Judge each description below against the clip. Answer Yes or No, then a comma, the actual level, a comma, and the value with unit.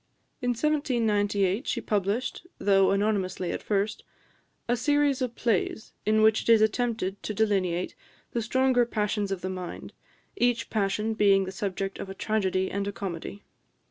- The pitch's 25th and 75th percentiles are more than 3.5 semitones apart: No, average, 3.2 semitones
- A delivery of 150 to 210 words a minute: Yes, average, 155 wpm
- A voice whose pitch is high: Yes, high, 210 Hz